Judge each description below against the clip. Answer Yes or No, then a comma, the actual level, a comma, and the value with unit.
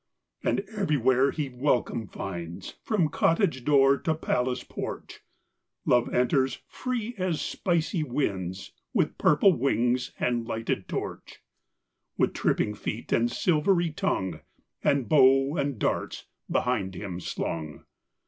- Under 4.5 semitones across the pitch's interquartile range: No, average, 5.2 semitones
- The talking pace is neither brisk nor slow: No, slow, 120 wpm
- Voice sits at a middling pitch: No, low, 130 Hz